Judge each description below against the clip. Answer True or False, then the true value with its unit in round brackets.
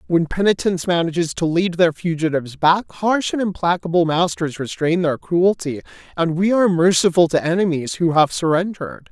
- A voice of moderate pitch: True (175 Hz)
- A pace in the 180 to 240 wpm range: False (160 wpm)